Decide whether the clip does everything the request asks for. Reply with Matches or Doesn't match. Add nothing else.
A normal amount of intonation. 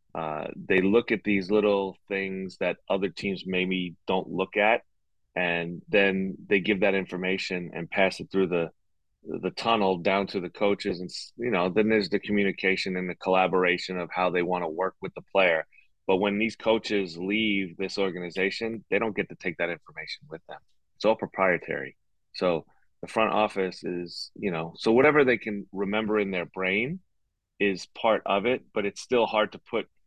Doesn't match